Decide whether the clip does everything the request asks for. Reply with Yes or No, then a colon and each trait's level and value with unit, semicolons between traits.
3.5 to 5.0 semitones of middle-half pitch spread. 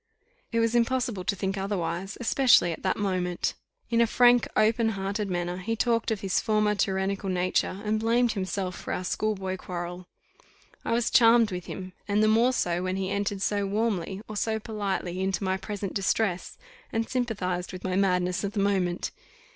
No: average, 3.1 semitones